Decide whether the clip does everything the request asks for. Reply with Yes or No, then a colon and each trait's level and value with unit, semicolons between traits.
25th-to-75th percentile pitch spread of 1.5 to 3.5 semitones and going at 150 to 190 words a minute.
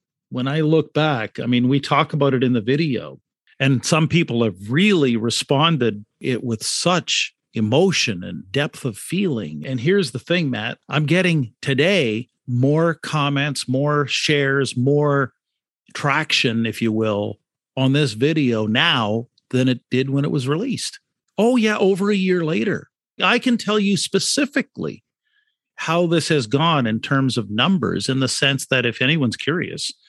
No: average, 5.1 semitones; average, 160 wpm